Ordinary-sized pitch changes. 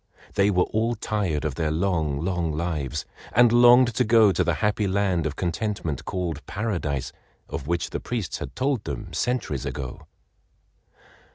No: wide, 5.8 semitones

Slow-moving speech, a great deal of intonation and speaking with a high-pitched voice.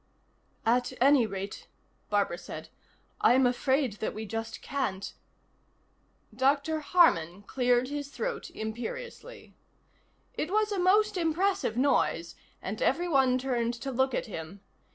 Yes: slow, 125 wpm; wide, 6.4 semitones; very high, 260 Hz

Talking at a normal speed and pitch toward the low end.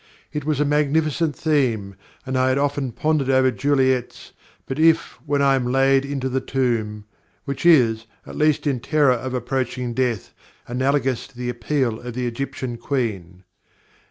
Yes: average, 160 wpm; low, 130 Hz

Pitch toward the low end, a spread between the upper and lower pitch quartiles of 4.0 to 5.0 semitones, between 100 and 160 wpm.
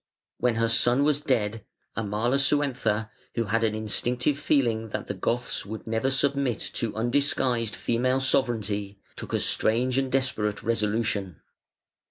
No: low, 115 Hz; average, 3.2 semitones; slow, 135 wpm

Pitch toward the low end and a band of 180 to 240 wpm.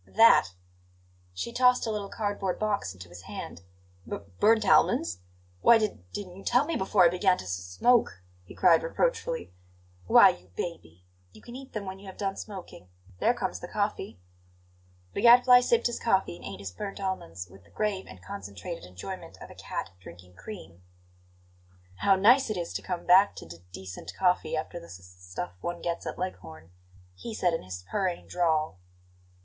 No: medium, 175 Hz; average, 185 wpm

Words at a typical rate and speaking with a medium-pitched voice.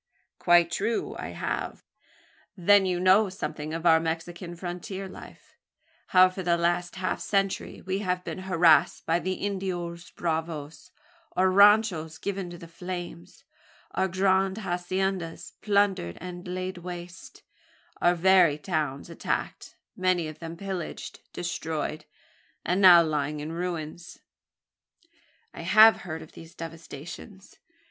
No: slow, 130 wpm; medium, 175 Hz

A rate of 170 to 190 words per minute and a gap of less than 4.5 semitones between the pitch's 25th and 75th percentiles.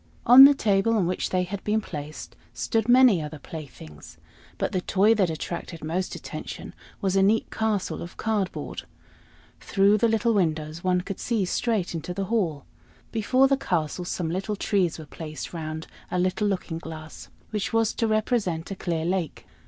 No: average, 175 wpm; average, 4.8 semitones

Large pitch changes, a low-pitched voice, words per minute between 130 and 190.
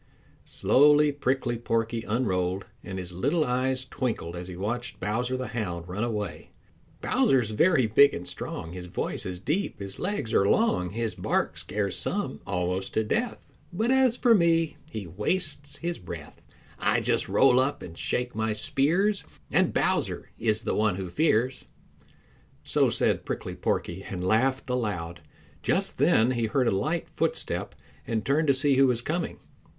Yes: wide, 6.4 semitones; low, 120 Hz; average, 165 wpm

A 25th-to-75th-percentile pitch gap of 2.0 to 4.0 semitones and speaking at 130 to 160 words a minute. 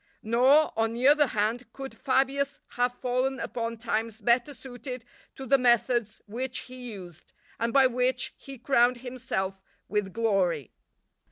Yes: narrow, 2.6 semitones; average, 145 wpm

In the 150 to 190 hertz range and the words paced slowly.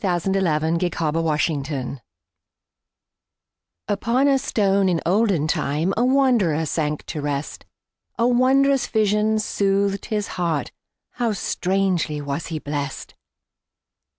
Yes: medium, 185 Hz; slow, 95 wpm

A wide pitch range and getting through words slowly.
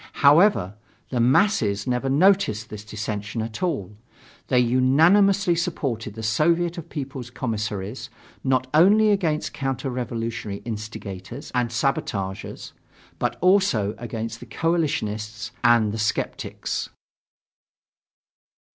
Yes: wide, 6.7 semitones; slow, 105 wpm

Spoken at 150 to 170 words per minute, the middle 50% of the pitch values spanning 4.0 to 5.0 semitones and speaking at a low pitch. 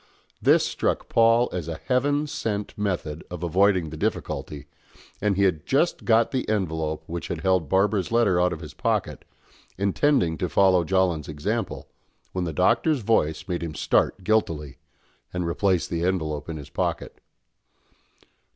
Yes: average, 155 wpm; average, 4.5 semitones; very low, 90 Hz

